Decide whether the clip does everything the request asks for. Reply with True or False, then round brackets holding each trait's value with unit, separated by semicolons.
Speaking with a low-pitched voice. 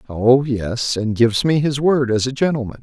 True (125 Hz)